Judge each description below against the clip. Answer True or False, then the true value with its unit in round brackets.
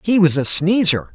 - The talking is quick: True (210 wpm)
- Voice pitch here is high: False (175 Hz)